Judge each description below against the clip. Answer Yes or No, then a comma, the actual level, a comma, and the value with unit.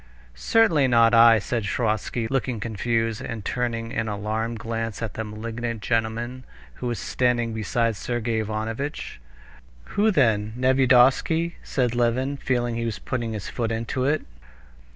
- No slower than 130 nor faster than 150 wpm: Yes, average, 140 wpm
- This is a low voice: Yes, low, 115 Hz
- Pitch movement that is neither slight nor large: No, narrow, 2.0 semitones